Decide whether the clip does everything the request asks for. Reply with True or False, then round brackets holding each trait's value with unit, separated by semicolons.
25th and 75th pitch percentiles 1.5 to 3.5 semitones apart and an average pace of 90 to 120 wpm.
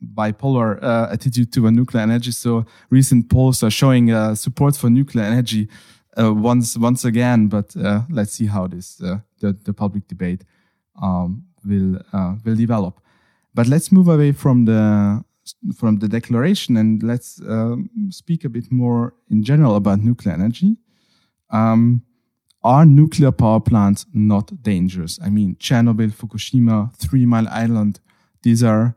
False (2.7 semitones; 155 wpm)